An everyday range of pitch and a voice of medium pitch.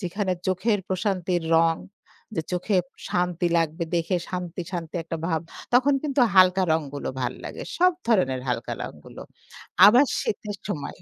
Yes: average, 3.7 semitones; medium, 180 Hz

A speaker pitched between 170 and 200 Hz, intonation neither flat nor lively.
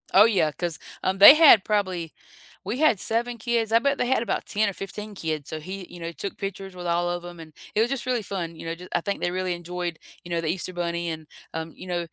Yes: medium, 185 Hz; average, 3.9 semitones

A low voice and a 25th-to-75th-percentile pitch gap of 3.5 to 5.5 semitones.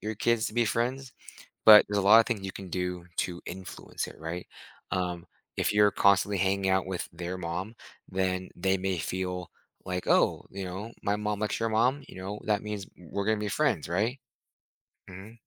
No: very low, 95 Hz; average, 2.7 semitones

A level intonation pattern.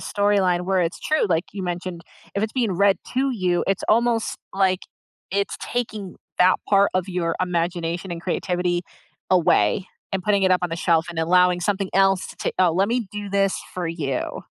Yes: narrow, 2.3 semitones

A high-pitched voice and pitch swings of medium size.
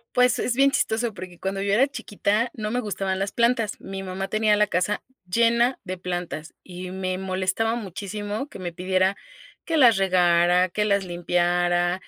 Yes: high, 195 Hz; average, 3.3 semitones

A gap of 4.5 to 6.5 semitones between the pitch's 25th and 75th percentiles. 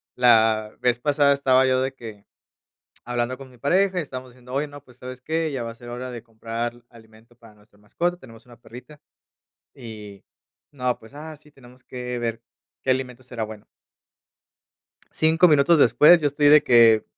No: average, 3.4 semitones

